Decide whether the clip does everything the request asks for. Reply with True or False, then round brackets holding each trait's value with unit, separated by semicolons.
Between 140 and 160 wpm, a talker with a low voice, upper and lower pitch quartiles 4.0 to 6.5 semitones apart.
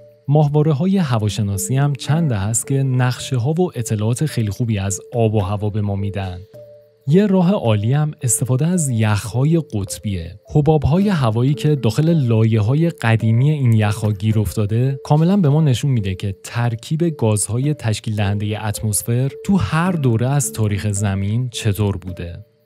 True (150 wpm; 120 Hz; 5.6 semitones)